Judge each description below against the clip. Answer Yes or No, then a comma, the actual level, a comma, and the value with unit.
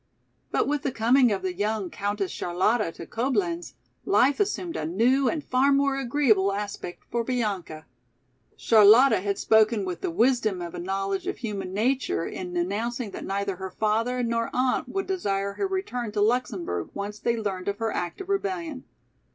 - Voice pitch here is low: No, high, 215 Hz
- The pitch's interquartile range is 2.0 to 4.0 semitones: No, average, 4.6 semitones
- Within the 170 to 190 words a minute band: Yes, average, 175 wpm